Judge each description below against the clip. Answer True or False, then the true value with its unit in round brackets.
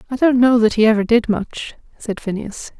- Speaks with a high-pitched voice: True (225 Hz)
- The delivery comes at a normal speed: False (215 wpm)